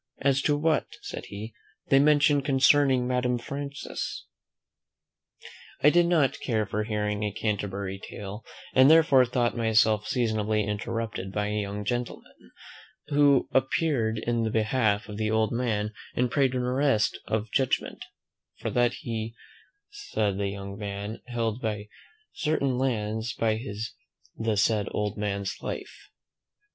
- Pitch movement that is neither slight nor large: Yes, average, 3.9 semitones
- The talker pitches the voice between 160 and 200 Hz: No, low, 115 Hz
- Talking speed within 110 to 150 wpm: Yes, average, 140 wpm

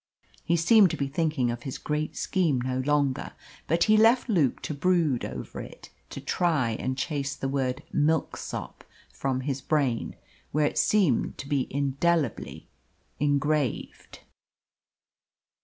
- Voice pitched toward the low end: No, medium, 145 Hz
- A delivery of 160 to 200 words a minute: No, average, 140 wpm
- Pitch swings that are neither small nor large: Yes, average, 3.8 semitones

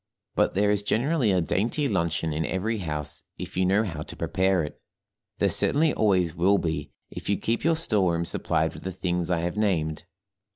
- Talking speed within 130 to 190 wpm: No, average, 200 wpm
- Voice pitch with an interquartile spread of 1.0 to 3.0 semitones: No, average, 4.0 semitones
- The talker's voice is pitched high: No, very low, 95 Hz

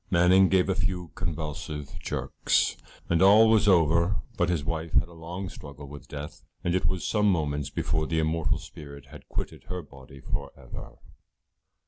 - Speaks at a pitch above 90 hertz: No, very low, 85 Hz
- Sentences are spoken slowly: No, average, 170 wpm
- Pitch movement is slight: No, average, 3.5 semitones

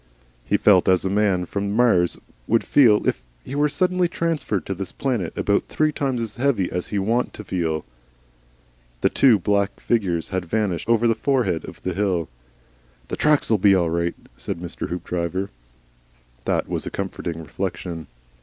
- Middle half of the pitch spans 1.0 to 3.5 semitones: No, average, 5.0 semitones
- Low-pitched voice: Yes, low, 100 Hz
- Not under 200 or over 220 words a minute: No, average, 175 wpm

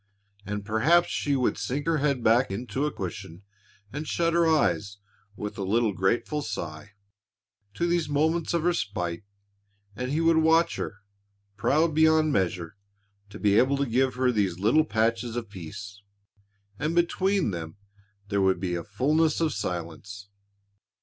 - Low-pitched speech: Yes, low, 120 Hz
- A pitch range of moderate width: No, wide, 7.6 semitones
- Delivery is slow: No, average, 155 wpm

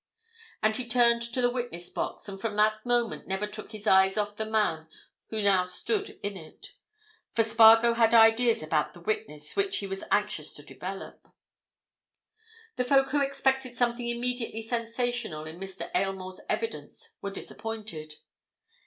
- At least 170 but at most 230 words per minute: No, average, 155 wpm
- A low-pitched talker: No, high, 220 Hz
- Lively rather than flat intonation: No, average, 3.8 semitones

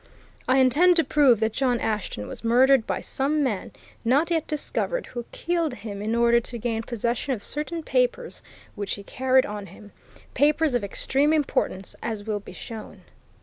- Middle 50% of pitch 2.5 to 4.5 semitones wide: No, average, 5.2 semitones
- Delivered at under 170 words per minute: No, average, 175 wpm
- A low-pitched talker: No, very high, 250 Hz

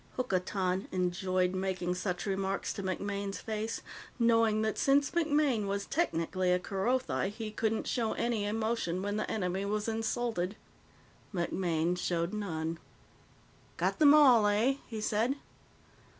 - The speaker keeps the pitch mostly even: No, average, 3.7 semitones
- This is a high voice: Yes, high, 205 Hz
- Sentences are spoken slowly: Yes, slow, 130 wpm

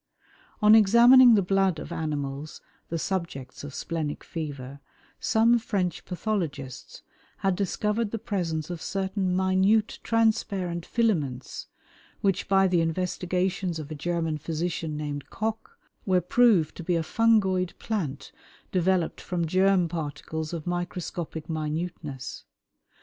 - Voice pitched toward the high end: No, medium, 180 Hz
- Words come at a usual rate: No, slow, 120 wpm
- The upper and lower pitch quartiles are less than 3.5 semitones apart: No, average, 3.8 semitones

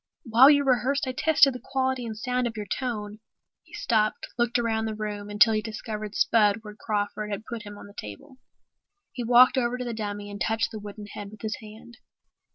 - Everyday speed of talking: No, fast, 210 wpm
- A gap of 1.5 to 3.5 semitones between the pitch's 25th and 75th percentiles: Yes, average, 2.7 semitones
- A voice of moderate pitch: No, high, 220 Hz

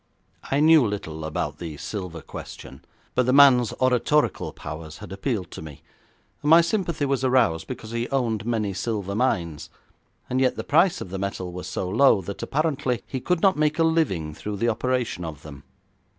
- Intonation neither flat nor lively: No, wide, 7.2 semitones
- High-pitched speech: No, low, 115 Hz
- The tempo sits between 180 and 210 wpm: Yes, average, 185 wpm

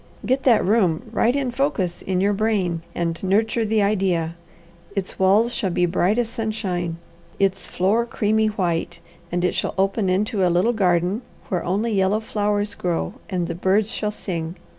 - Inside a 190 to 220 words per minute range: No, average, 170 wpm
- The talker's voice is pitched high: Yes, high, 195 Hz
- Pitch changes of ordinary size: Yes, average, 3.4 semitones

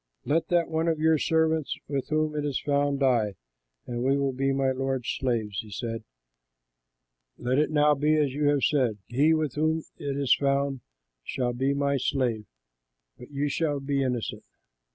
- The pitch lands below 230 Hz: Yes, medium, 140 Hz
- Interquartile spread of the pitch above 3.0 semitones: No, average, 2.7 semitones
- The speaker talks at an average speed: Yes, average, 175 wpm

